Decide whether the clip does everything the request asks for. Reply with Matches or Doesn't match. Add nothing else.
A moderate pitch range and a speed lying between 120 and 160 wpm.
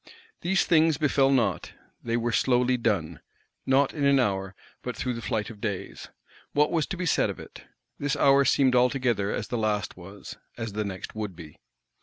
Doesn't match